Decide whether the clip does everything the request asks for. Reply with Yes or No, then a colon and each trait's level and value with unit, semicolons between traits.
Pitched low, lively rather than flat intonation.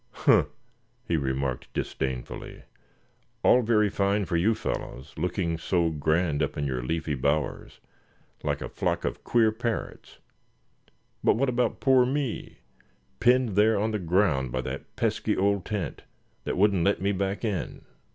Yes: very low, 95 Hz; wide, 5.7 semitones